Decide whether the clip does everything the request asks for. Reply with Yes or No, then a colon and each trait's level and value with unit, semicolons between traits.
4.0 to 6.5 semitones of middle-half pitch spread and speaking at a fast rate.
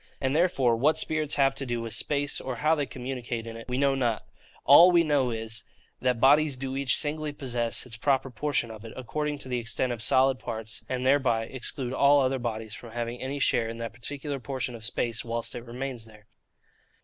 No: average, 3.2 semitones; fast, 215 wpm